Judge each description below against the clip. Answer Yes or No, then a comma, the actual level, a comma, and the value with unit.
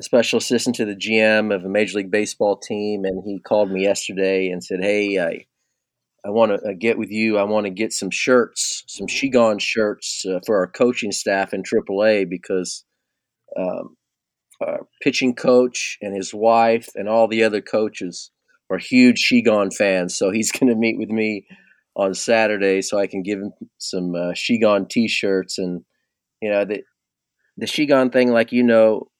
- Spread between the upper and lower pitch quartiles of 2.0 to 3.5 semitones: Yes, average, 2.7 semitones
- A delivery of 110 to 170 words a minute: No, average, 180 wpm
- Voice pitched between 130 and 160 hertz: No, low, 105 Hz